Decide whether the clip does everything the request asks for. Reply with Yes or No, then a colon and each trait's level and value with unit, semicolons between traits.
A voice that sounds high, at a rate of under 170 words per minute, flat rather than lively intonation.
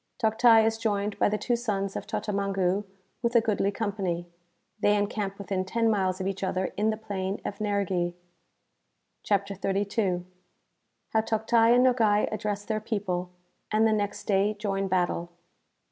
Yes: high, 205 Hz; average, 155 wpm; narrow, 2.1 semitones